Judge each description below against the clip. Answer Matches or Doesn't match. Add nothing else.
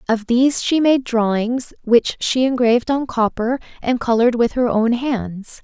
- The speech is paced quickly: Doesn't match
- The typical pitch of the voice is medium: Doesn't match